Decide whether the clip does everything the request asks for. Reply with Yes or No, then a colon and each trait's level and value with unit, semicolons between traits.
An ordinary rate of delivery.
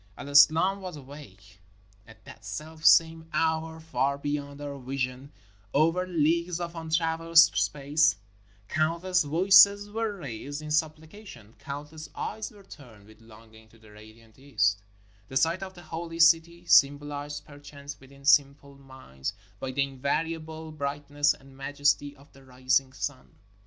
Yes: average, 145 wpm